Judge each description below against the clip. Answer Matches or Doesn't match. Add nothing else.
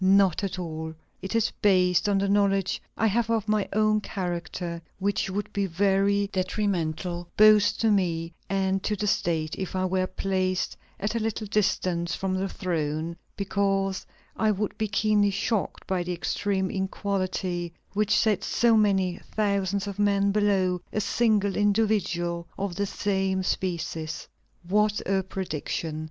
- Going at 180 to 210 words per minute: Doesn't match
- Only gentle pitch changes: Matches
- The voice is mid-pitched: Doesn't match